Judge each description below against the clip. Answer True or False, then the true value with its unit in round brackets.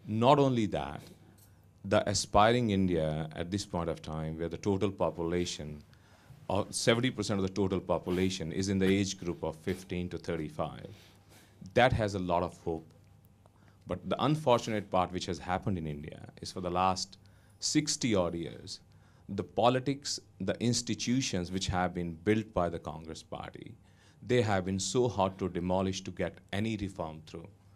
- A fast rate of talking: False (165 wpm)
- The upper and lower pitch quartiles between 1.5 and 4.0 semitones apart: True (3.4 semitones)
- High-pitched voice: False (95 Hz)